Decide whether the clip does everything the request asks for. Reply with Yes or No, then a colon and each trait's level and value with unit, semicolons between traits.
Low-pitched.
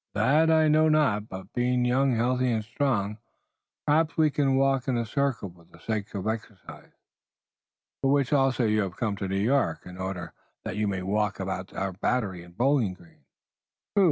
Yes: low, 115 Hz